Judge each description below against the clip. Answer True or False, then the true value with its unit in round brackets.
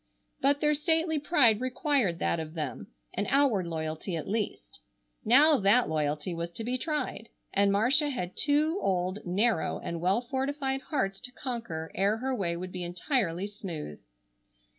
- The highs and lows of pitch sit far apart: True (7.4 semitones)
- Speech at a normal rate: True (160 wpm)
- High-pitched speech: True (210 Hz)